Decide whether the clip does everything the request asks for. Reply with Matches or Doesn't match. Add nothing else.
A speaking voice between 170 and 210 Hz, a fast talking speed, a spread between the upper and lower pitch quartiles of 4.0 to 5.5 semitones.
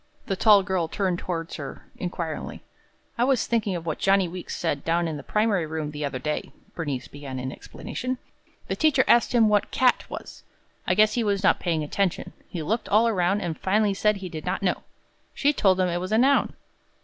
Matches